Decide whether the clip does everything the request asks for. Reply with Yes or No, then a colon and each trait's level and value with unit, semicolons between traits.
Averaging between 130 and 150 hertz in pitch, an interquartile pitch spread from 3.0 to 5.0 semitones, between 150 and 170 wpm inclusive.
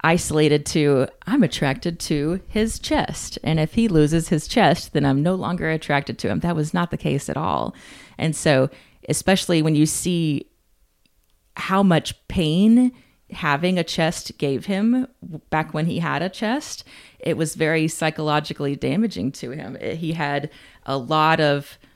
No: medium, 160 Hz; average, 3.3 semitones; average, 160 wpm